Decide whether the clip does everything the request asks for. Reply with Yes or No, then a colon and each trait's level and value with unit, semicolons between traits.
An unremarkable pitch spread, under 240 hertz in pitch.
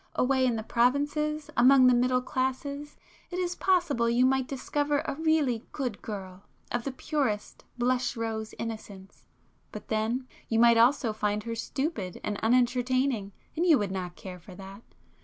No: average, 4.0 semitones; high, 245 Hz